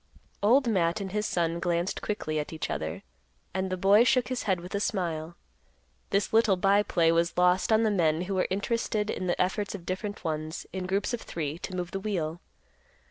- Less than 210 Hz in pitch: Yes, medium, 185 Hz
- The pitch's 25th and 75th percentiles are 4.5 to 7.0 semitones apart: No, average, 3.3 semitones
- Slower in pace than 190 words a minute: No, fast, 205 wpm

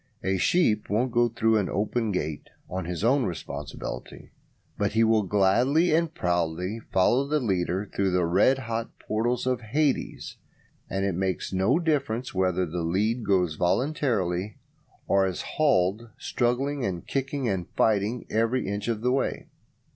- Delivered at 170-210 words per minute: No, average, 155 wpm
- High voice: No, low, 110 Hz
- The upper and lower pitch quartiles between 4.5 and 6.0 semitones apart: Yes, average, 5.0 semitones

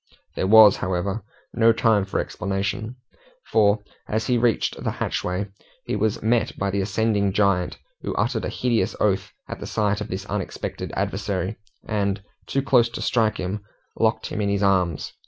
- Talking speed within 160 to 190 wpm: Yes, average, 170 wpm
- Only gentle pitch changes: Yes, narrow, 2.2 semitones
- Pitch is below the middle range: Yes, low, 105 Hz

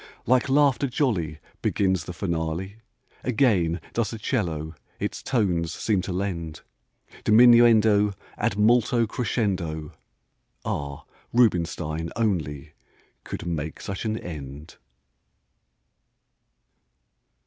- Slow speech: Yes, slow, 95 wpm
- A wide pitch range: Yes, wide, 5.8 semitones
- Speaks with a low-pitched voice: Yes, very low, 95 Hz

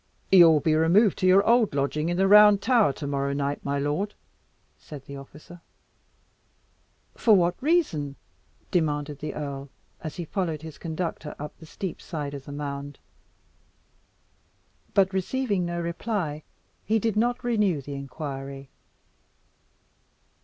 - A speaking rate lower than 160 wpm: Yes, average, 140 wpm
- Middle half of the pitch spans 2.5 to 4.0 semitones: No, wide, 5.4 semitones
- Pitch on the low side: No, medium, 160 Hz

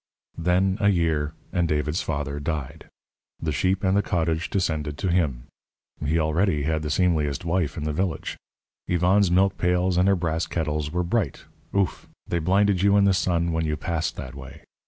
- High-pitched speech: No, very low, 85 Hz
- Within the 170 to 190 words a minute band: Yes, average, 180 wpm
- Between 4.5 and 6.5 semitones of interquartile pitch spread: No, average, 3.3 semitones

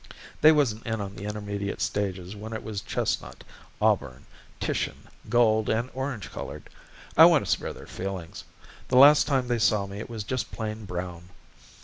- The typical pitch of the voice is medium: No, low, 105 Hz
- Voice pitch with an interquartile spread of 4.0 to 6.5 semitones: No, average, 3.3 semitones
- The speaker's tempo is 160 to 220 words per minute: Yes, average, 170 wpm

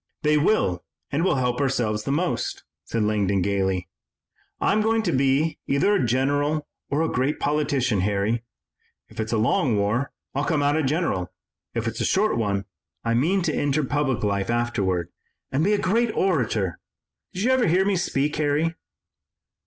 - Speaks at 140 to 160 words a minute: No, average, 170 wpm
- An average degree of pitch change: No, wide, 6.6 semitones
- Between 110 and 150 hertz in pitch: Yes, low, 135 Hz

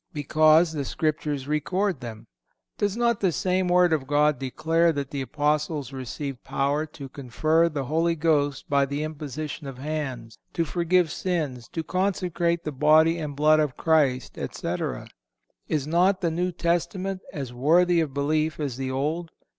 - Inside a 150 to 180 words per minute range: Yes, average, 160 wpm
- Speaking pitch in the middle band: Yes, medium, 155 Hz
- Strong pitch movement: No, average, 3.1 semitones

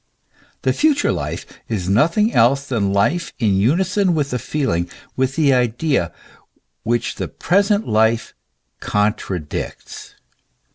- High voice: No, low, 125 Hz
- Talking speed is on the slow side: Yes, slow, 115 wpm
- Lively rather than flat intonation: Yes, wide, 8.0 semitones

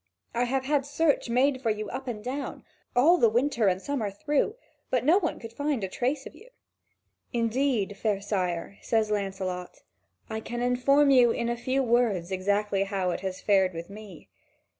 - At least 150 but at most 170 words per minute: No, average, 185 wpm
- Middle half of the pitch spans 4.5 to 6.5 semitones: Yes, average, 5.1 semitones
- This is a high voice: Yes, high, 230 Hz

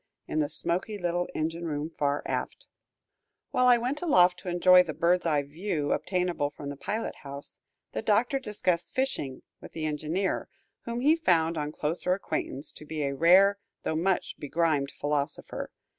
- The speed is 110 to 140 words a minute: No, average, 165 wpm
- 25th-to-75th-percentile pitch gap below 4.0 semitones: No, average, 4.4 semitones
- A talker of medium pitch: Yes, medium, 170 Hz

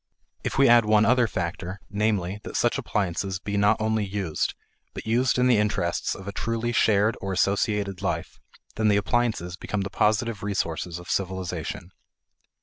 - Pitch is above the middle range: No, low, 100 Hz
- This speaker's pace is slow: No, average, 165 wpm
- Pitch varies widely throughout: No, narrow, 2.6 semitones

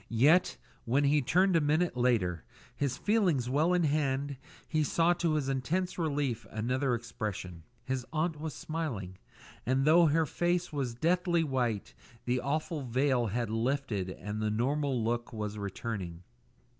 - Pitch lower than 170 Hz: Yes, low, 135 Hz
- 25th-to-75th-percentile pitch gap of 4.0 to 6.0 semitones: Yes, average, 5.2 semitones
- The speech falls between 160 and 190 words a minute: No, average, 150 wpm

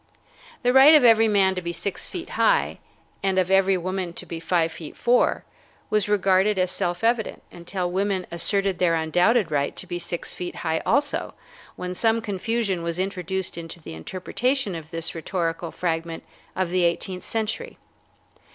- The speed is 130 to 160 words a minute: No, average, 170 wpm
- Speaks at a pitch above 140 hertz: Yes, medium, 185 Hz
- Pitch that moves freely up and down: No, average, 3.4 semitones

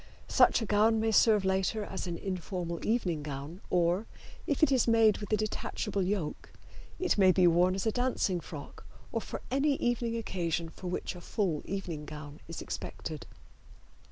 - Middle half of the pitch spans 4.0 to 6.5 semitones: Yes, average, 4.5 semitones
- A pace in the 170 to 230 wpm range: Yes, average, 175 wpm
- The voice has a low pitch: No, high, 190 Hz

